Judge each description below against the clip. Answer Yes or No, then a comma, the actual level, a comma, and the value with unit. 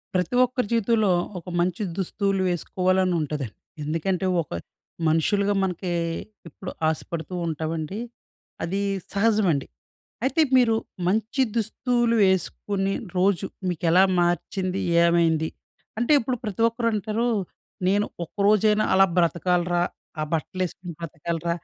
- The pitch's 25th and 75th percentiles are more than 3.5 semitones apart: Yes, average, 3.9 semitones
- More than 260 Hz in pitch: No, medium, 185 Hz